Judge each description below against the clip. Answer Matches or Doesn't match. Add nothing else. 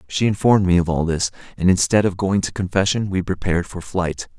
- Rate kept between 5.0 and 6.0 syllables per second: Matches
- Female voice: Doesn't match